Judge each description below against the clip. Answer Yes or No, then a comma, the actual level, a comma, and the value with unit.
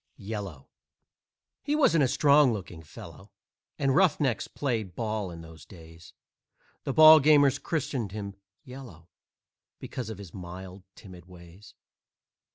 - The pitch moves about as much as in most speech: No, wide, 7.3 semitones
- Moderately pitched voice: No, low, 105 Hz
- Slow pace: Yes, slow, 120 wpm